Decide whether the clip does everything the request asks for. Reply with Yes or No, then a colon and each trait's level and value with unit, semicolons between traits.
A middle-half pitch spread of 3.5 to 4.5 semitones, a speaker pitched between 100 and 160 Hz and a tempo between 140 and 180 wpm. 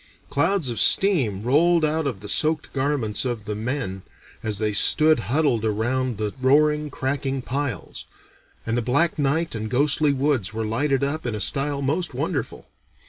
No: average, 5.0 semitones; low, 135 Hz; average, 165 wpm